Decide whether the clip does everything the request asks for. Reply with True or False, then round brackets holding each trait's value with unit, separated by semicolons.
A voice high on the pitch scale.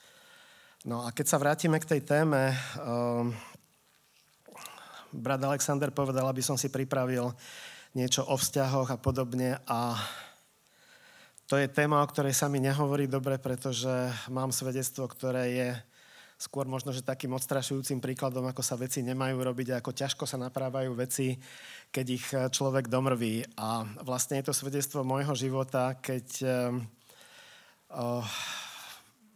False (130 Hz)